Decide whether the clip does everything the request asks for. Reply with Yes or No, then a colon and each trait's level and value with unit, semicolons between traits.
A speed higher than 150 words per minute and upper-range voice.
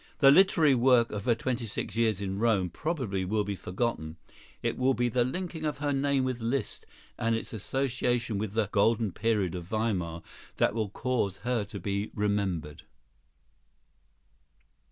No: average, 160 wpm; low, 115 Hz